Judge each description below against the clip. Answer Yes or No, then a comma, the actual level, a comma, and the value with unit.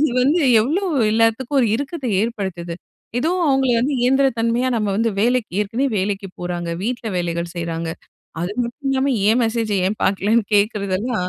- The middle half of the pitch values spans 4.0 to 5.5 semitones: Yes, average, 4.7 semitones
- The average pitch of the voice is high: Yes, high, 225 Hz